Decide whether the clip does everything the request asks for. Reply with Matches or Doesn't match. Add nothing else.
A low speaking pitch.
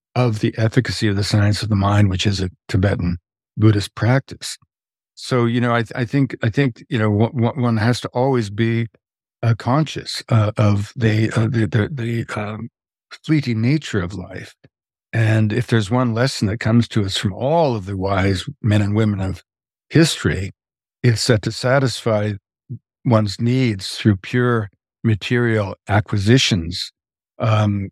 Matches